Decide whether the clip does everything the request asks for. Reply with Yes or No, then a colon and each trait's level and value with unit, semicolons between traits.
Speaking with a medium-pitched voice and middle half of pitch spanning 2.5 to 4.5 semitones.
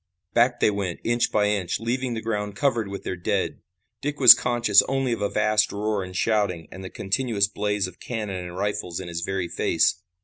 No: low, 105 Hz; average, 3.6 semitones